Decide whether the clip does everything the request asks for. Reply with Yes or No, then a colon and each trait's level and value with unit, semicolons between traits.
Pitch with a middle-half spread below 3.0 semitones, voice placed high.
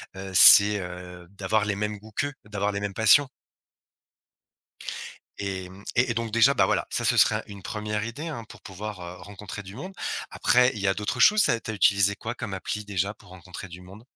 No: narrow, 2.6 semitones; low, 100 Hz